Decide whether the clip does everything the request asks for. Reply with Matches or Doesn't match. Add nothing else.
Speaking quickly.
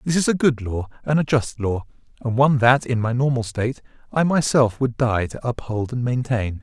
Matches